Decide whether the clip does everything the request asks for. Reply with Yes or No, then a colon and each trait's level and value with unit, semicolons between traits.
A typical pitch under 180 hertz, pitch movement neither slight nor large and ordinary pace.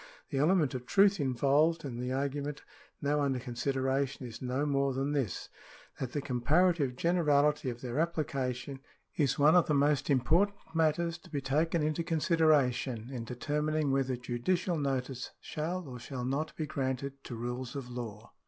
Yes: medium, 140 Hz; average, 3.4 semitones; average, 160 wpm